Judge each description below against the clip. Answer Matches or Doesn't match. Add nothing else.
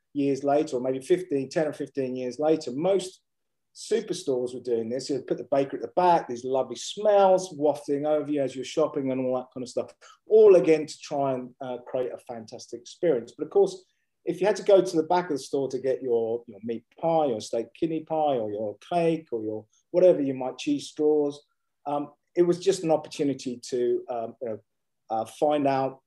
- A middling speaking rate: Doesn't match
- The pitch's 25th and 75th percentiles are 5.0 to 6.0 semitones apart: Matches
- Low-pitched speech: Doesn't match